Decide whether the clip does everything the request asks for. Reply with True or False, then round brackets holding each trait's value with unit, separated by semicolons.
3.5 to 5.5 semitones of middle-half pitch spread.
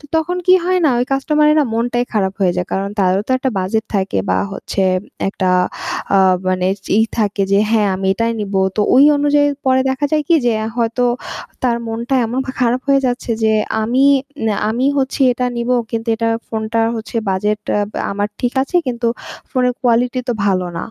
True (4.1 semitones)